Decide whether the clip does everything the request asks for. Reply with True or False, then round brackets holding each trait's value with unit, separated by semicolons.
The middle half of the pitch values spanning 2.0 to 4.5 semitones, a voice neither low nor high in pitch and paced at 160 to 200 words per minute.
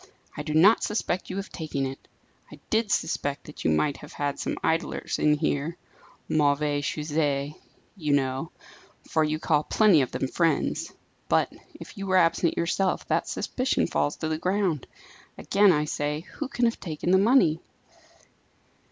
True (4.2 semitones; 155 Hz; 165 wpm)